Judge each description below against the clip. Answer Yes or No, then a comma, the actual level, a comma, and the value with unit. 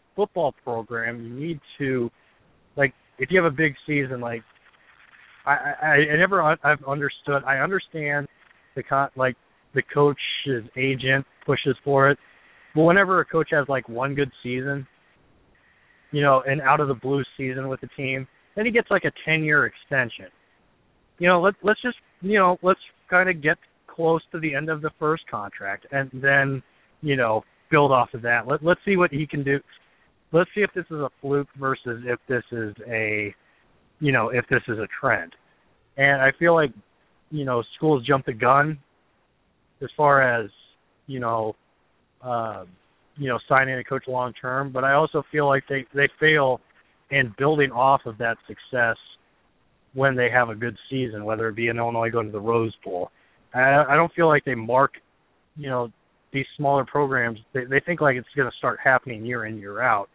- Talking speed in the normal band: Yes, average, 190 wpm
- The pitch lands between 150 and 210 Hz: No, low, 135 Hz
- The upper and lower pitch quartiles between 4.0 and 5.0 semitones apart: No, average, 3.6 semitones